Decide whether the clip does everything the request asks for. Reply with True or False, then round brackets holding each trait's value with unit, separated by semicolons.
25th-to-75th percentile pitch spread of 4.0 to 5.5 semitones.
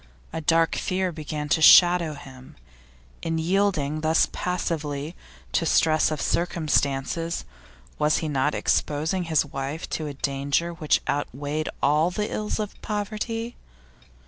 False (3.1 semitones)